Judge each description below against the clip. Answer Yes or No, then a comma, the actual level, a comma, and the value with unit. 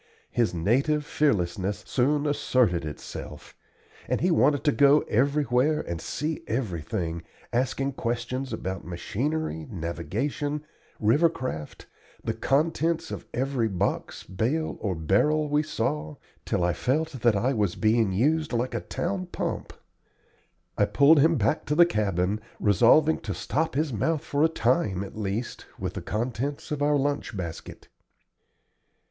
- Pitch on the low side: Yes, low, 125 Hz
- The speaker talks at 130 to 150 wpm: Yes, average, 140 wpm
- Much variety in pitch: Yes, wide, 7.0 semitones